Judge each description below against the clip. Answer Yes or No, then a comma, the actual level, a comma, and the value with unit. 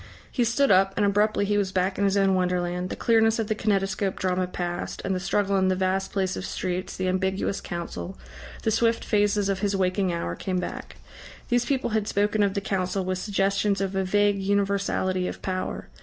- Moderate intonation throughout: No, narrow, 1.7 semitones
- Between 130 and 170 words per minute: No, fast, 205 wpm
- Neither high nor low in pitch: No, high, 195 Hz